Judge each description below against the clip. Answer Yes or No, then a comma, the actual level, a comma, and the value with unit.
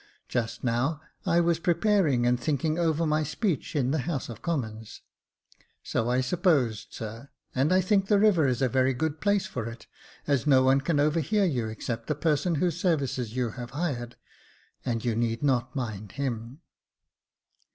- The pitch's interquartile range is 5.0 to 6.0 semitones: Yes, wide, 5.4 semitones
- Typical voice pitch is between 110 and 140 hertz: Yes, low, 135 Hz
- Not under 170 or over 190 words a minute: Yes, average, 180 wpm